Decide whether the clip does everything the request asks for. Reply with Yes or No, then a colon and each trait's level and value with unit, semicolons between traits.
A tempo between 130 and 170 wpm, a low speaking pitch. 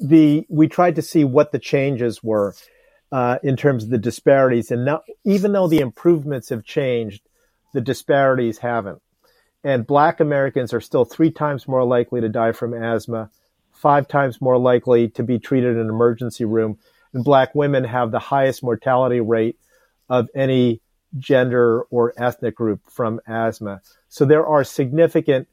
Yes: average, 165 wpm; low, 125 Hz